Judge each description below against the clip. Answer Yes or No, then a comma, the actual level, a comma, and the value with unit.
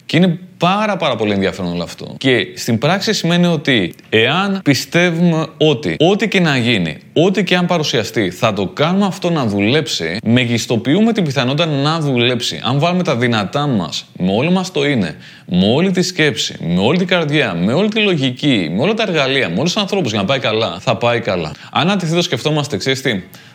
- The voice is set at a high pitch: No, medium, 155 Hz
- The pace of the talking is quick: Yes, fast, 195 wpm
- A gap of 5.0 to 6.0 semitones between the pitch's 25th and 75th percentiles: Yes, wide, 5.4 semitones